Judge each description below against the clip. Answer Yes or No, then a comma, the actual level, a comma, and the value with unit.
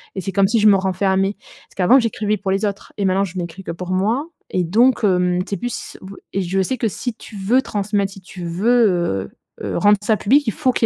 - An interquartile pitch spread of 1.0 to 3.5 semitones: Yes, average, 2.9 semitones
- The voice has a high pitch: Yes, high, 195 Hz